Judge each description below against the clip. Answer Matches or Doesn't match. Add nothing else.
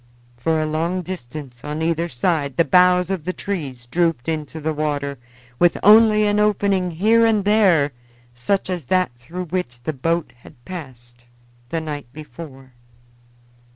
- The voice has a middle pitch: Matches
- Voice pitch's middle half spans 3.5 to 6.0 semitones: Matches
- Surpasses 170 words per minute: Doesn't match